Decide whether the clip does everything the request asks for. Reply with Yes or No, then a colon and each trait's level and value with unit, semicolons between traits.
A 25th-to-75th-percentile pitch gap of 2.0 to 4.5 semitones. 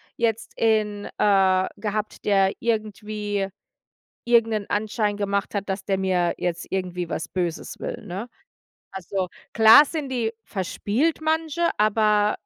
Yes: narrow, 2.6 semitones